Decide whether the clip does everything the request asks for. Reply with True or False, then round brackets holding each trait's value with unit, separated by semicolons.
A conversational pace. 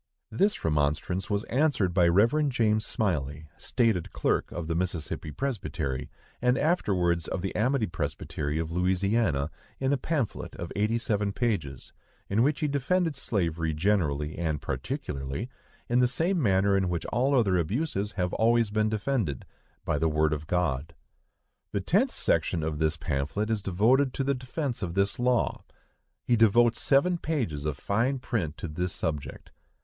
True (155 wpm)